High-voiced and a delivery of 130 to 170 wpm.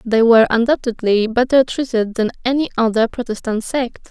Yes: high, 235 Hz; average, 145 wpm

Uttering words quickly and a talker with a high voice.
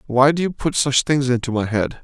No: fast, 265 wpm; low, 135 Hz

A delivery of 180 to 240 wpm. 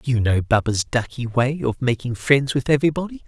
Yes: average, 185 wpm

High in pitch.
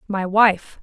Yes: high, 200 Hz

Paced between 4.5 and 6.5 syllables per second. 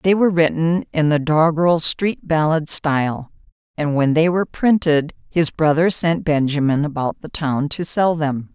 Yes: 4.6 syllables/s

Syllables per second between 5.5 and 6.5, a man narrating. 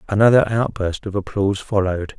Yes: 6.0 syllables/s; male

